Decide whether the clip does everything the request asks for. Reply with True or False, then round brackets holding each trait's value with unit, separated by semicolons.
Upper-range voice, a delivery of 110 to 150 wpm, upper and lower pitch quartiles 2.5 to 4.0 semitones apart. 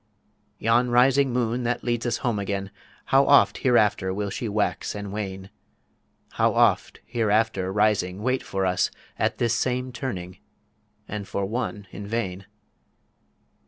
False (110 Hz; 140 wpm; 3.7 semitones)